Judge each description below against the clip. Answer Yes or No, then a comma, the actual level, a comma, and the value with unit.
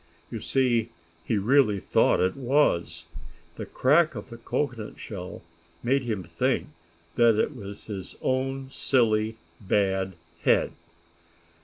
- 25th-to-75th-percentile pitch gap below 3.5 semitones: No, average, 5.0 semitones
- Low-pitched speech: Yes, low, 115 Hz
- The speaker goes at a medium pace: No, slow, 125 wpm